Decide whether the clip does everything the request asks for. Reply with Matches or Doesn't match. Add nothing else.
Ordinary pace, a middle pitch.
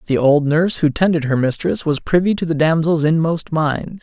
Doesn't match